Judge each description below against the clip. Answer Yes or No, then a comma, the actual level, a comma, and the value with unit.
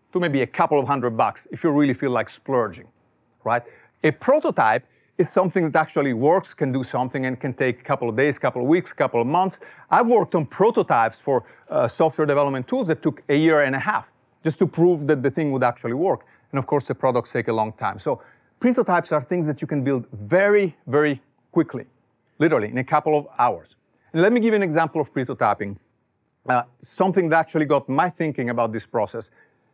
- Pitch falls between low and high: Yes, medium, 145 Hz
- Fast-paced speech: Yes, fast, 220 wpm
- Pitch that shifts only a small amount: No, average, 4.3 semitones